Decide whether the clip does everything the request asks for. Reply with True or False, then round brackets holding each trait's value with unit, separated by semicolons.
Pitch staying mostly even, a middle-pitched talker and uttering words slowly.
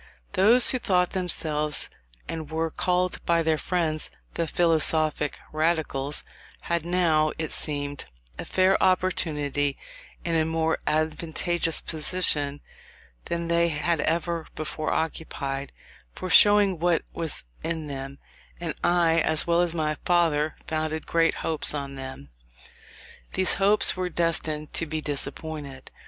True (2.2 semitones; 160 Hz; 130 wpm)